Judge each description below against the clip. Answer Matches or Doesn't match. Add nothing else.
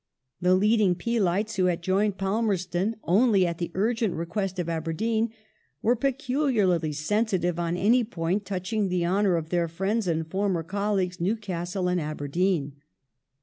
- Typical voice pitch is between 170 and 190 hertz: Matches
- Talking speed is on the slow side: Doesn't match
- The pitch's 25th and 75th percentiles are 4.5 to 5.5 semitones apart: Doesn't match